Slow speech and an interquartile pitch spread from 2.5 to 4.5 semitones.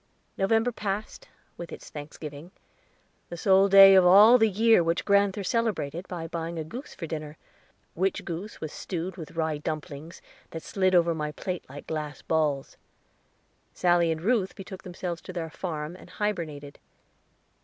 No: average, 155 wpm; average, 3.5 semitones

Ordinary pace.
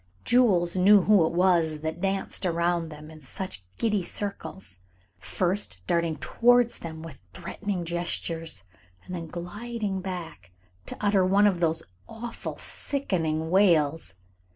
No: slow, 130 wpm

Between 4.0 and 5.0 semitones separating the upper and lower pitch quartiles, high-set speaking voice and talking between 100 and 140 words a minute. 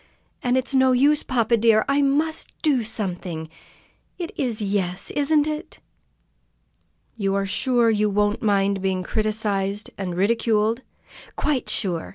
Yes: average, 4.7 semitones; high, 220 Hz; slow, 135 wpm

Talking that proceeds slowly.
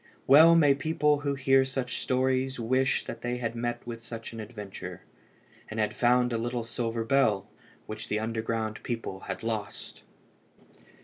No: average, 160 wpm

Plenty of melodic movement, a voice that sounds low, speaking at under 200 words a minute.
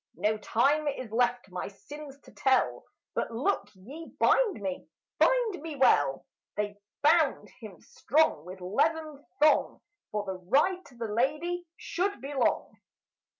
No: wide, 7.1 semitones; very high, 265 Hz; average, 145 wpm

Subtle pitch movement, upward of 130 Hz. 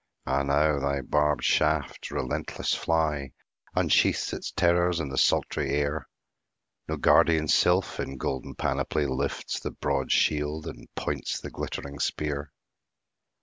No: narrow, 1.9 semitones; very low, 75 Hz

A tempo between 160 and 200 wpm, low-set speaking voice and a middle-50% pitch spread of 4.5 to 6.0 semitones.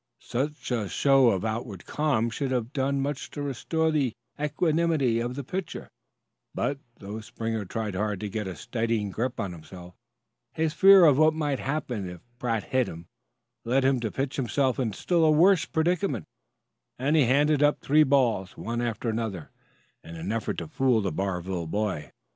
Yes: average, 175 wpm; low, 125 Hz; wide, 5.6 semitones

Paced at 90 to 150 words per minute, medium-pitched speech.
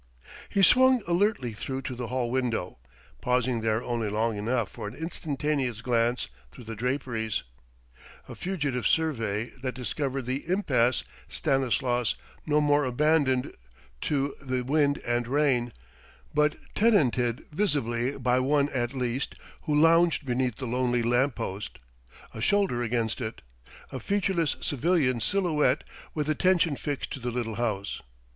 No: average, 140 wpm; low, 130 Hz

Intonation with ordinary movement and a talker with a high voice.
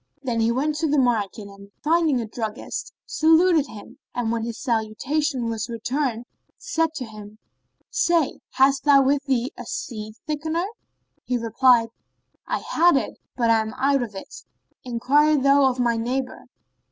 Yes: average, 4.4 semitones; very high, 255 Hz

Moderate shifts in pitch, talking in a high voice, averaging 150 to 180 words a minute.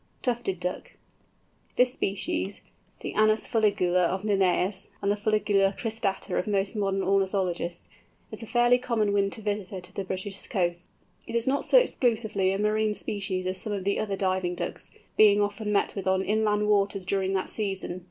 No: narrow, 2.1 semitones; high, 200 Hz; average, 170 wpm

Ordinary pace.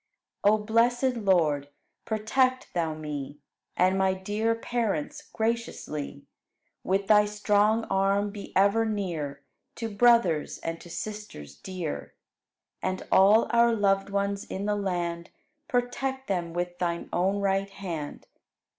No: slow, 130 wpm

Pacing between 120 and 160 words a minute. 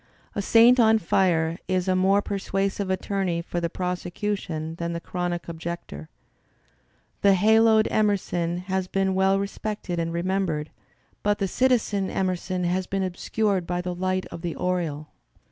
Yes: average, 150 wpm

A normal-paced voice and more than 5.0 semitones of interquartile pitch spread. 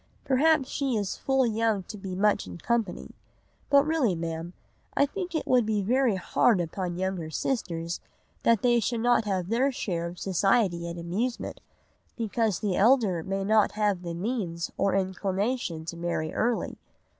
Yes: average, 165 wpm; wide, 5.4 semitones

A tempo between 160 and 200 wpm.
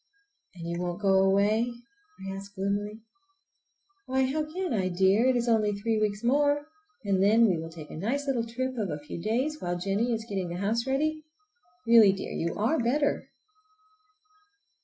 Yes: average, 180 wpm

